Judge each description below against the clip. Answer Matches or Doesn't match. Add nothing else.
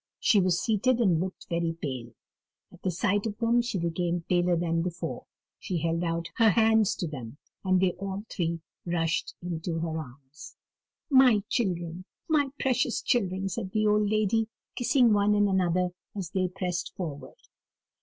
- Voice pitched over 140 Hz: Matches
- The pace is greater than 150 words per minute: Matches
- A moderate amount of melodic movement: Matches